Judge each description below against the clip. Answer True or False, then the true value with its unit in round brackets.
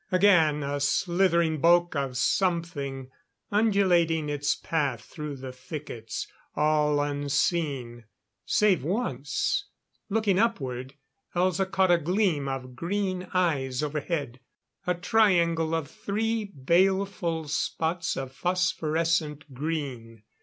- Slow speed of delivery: True (105 wpm)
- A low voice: False (160 Hz)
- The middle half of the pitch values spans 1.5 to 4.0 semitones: False (4.6 semitones)